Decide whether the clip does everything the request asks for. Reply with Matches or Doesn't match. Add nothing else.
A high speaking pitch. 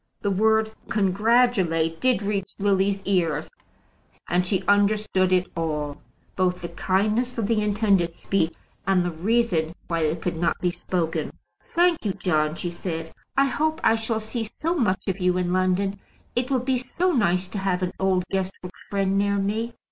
Matches